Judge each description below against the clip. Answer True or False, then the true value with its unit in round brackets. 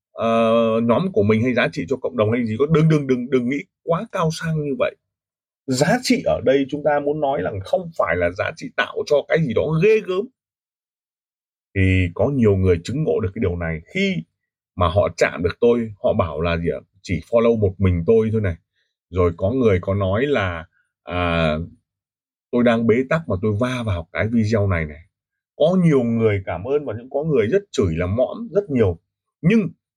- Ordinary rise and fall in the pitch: False (7.5 semitones)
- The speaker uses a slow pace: False (215 wpm)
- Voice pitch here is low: True (115 Hz)